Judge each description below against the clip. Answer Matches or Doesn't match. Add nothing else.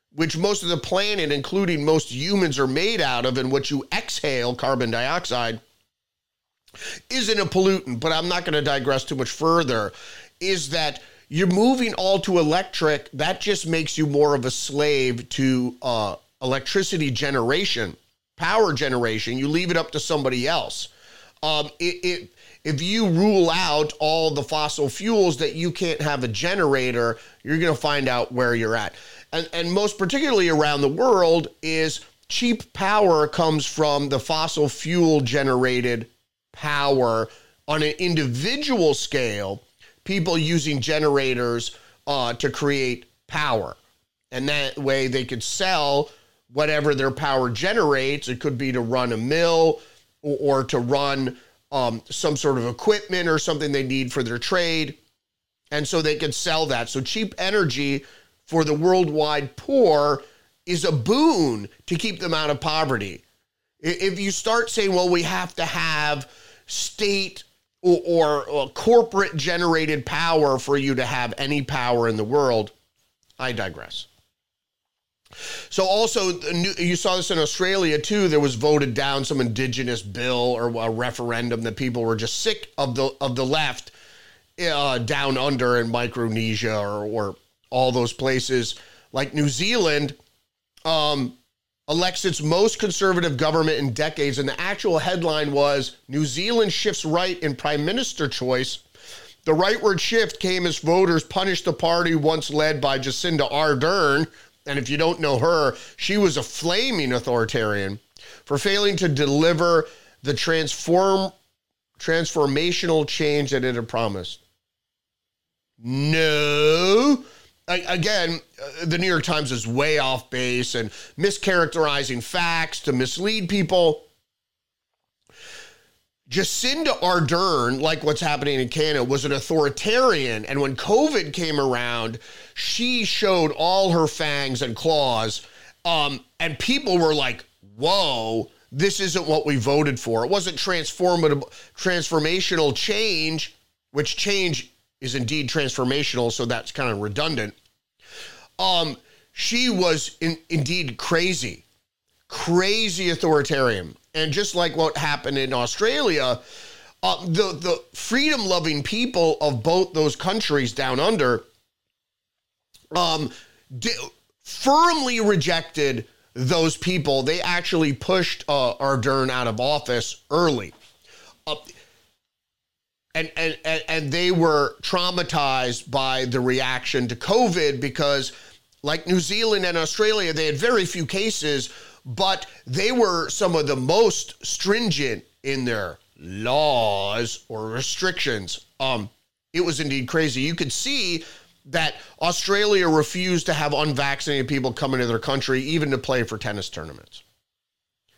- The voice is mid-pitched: Matches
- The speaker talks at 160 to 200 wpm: Doesn't match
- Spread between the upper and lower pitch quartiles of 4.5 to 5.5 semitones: Matches